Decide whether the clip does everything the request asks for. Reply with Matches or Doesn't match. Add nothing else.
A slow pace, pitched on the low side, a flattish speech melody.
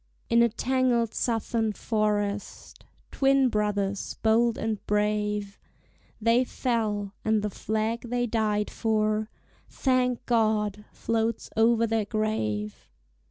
Doesn't match